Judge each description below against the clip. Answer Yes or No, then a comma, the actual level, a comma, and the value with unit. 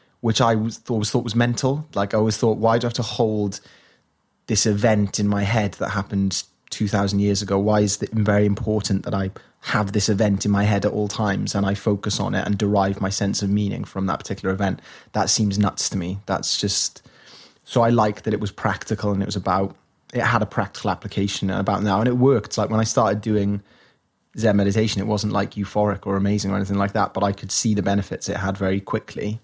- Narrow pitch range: Yes, narrow, 1.7 semitones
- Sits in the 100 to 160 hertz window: Yes, low, 105 Hz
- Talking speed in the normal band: No, fast, 230 wpm